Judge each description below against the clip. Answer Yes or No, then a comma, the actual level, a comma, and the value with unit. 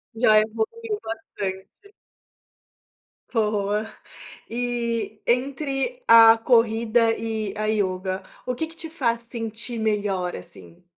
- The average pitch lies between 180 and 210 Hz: No, high, 225 Hz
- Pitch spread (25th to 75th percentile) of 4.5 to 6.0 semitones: No, narrow, 2.4 semitones